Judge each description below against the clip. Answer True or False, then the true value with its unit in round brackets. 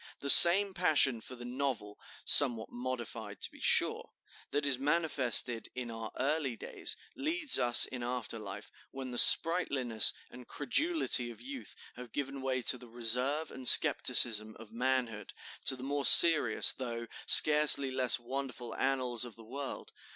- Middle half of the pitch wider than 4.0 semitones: False (3.0 semitones)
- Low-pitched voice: True (130 Hz)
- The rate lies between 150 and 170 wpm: True (155 wpm)